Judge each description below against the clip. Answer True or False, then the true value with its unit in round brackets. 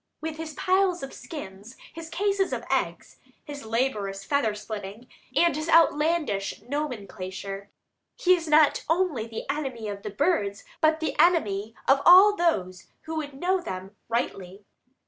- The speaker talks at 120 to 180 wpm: True (145 wpm)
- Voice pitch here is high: True (280 Hz)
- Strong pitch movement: True (8.2 semitones)